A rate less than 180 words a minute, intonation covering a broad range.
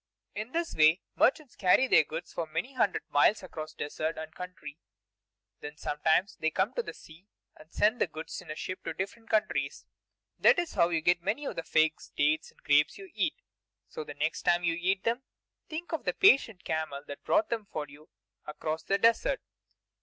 No: average, 195 wpm; wide, 6.6 semitones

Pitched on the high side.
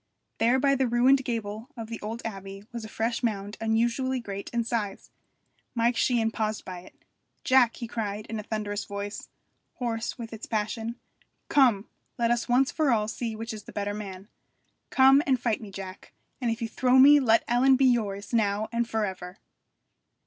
Yes: high, 225 Hz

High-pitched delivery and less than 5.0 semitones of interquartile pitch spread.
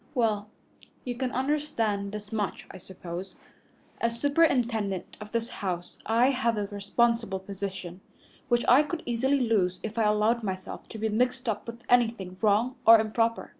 Yes: high, 225 Hz; average, 3.2 semitones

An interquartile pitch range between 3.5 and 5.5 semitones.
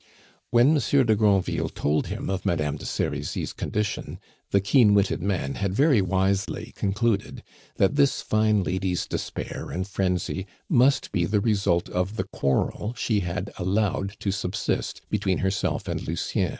No: average, 2.8 semitones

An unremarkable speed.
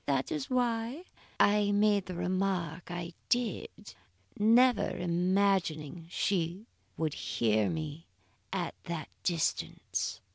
No: slow, 105 wpm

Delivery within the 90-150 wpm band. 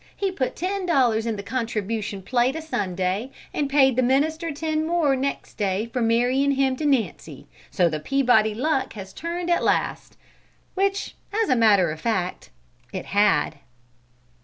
No: average, 160 wpm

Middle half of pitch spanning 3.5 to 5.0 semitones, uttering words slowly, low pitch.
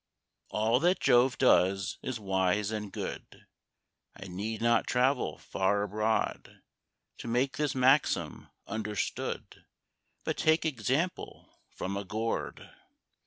Yes: average, 4.3 semitones; slow, 115 wpm; low, 110 Hz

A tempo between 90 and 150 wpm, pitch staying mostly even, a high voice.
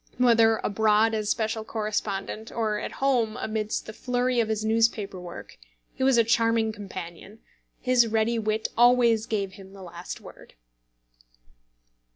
Yes: average, 145 wpm; narrow, 1.8 semitones; high, 220 Hz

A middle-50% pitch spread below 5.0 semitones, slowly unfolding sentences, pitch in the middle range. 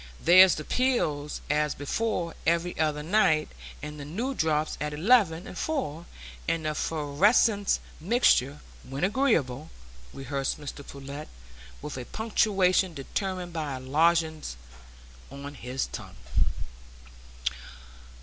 Yes: average, 4.6 semitones; slow, 115 wpm; medium, 155 Hz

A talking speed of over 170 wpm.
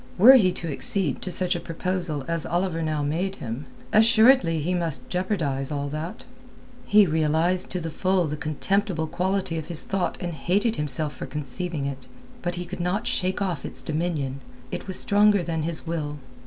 Yes: average, 180 wpm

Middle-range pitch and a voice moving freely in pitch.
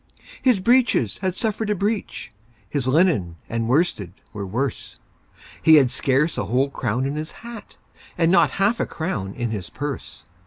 Yes: medium, 145 Hz; wide, 8.2 semitones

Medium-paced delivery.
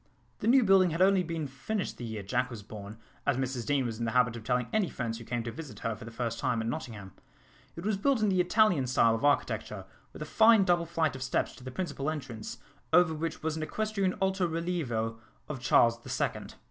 No: fast, 235 wpm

